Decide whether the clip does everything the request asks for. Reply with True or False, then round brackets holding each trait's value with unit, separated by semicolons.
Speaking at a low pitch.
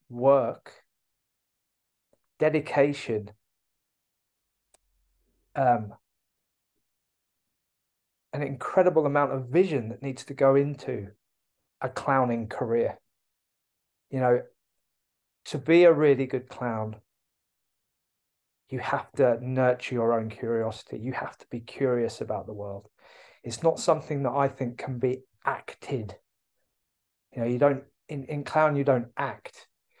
True (130 Hz)